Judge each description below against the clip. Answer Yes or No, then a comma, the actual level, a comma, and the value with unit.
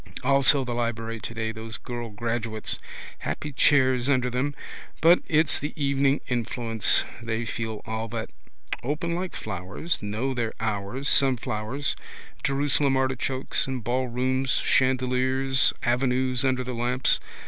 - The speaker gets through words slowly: Yes, slow, 125 wpm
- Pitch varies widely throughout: No, average, 2.8 semitones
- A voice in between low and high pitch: No, low, 125 Hz